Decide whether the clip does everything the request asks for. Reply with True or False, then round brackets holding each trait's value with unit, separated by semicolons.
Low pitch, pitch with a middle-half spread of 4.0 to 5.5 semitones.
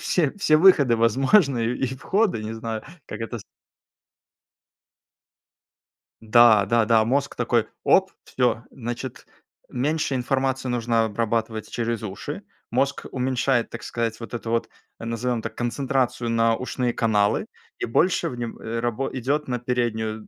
False (120 Hz; 2.6 semitones)